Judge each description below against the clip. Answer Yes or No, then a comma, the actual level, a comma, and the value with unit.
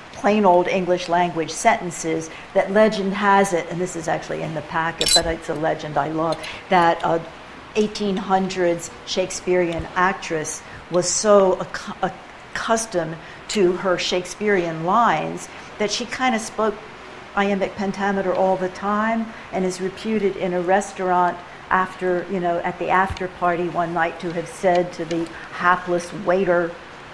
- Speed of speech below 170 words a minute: Yes, average, 145 wpm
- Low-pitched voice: No, medium, 180 Hz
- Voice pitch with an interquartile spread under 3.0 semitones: Yes, narrow, 2.4 semitones